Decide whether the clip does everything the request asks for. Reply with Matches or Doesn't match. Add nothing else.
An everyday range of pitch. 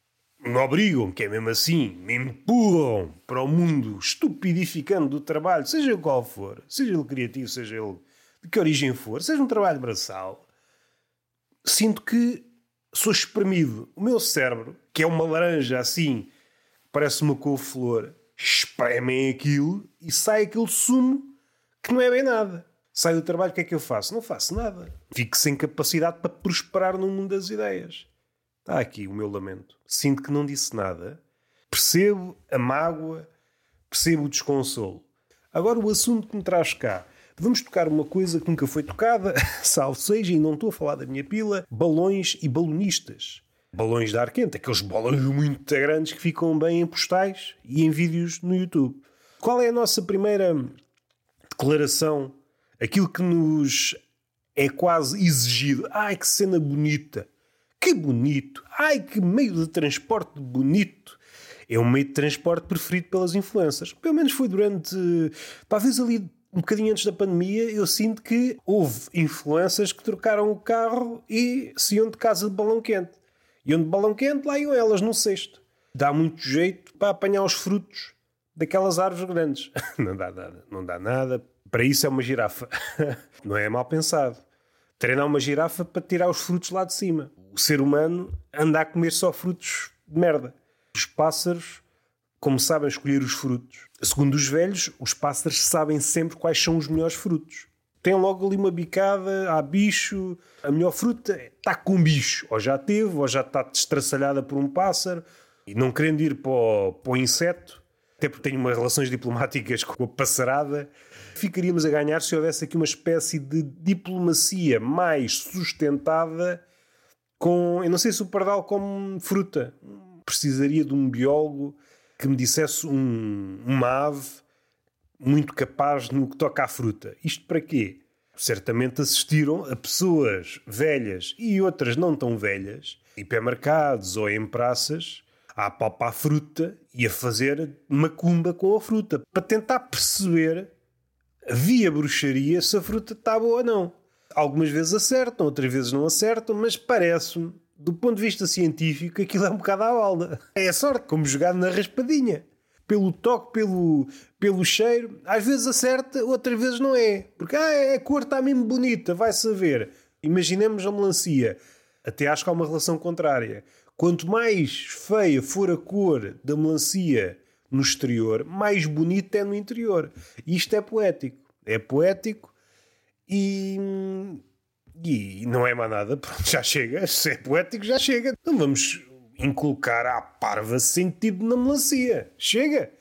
Doesn't match